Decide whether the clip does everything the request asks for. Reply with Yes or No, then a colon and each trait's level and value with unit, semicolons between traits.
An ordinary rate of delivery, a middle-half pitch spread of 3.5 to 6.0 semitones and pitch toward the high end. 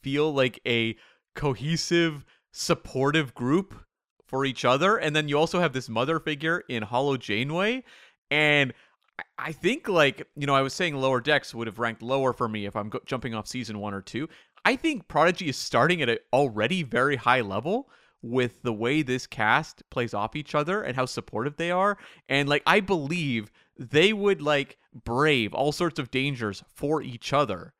No: average, 185 wpm; average, 4.4 semitones; low, 135 Hz